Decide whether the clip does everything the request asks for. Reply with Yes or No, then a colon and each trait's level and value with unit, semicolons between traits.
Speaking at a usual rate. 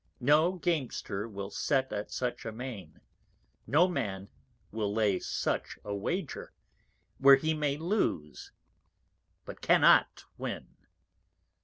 No: slow, 115 wpm